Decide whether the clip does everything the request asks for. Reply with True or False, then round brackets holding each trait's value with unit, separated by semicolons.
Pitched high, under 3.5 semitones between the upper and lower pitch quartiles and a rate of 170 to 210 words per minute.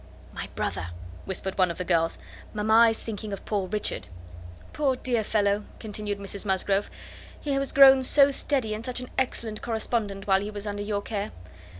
True (210 Hz; 2.9 semitones; 180 wpm)